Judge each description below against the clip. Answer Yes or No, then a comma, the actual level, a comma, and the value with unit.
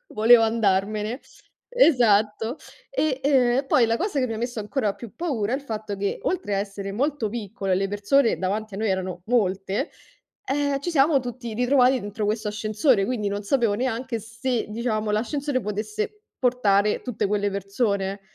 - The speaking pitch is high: Yes, high, 225 Hz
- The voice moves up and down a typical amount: Yes, average, 3.9 semitones